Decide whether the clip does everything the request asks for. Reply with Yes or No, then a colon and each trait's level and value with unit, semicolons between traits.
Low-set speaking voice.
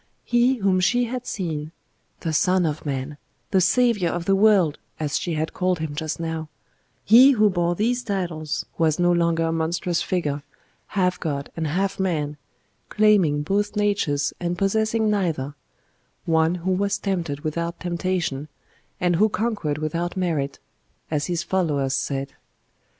No: medium, 175 Hz